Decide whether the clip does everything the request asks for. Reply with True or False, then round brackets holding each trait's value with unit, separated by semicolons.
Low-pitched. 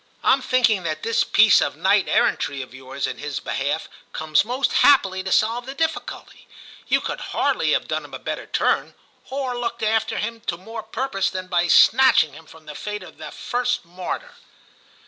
False (205 Hz)